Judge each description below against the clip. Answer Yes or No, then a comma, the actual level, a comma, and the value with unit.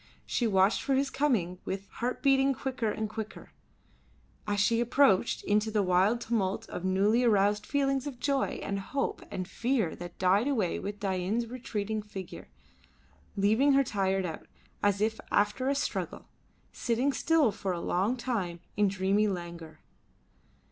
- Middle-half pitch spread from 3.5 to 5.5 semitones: Yes, average, 4.6 semitones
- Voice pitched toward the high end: Yes, high, 210 Hz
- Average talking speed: Yes, average, 155 wpm